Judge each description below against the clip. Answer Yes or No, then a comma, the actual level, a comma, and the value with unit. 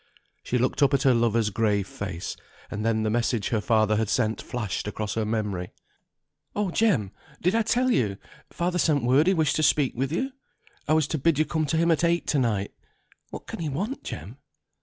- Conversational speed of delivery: No, fast, 210 wpm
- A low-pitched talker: Yes, low, 130 Hz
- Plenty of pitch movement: Yes, wide, 6.9 semitones